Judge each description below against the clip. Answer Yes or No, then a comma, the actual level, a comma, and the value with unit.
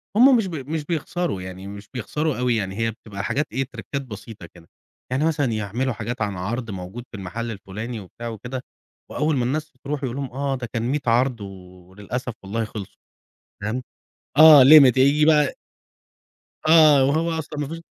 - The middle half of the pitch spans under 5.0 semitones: No, average, 5.3 semitones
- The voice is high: No, low, 125 Hz